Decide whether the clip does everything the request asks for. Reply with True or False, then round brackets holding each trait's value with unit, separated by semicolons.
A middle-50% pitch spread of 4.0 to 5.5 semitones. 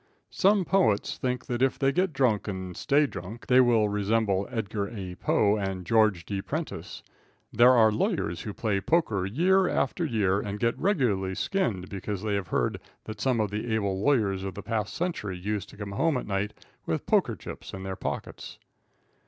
True (4.4 semitones)